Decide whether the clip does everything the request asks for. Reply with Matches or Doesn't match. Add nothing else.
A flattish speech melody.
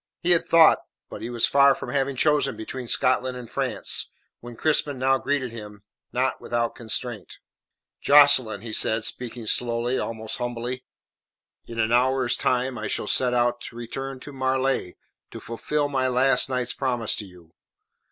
Matches